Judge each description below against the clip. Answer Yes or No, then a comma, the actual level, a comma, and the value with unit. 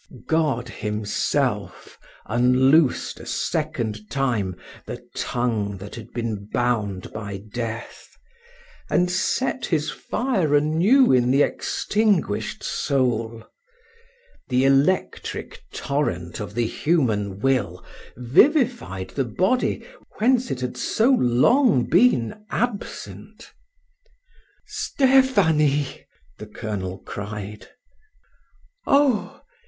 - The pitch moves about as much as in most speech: No, wide, 8.6 semitones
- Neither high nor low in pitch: No, low, 125 Hz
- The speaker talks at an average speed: No, slow, 90 wpm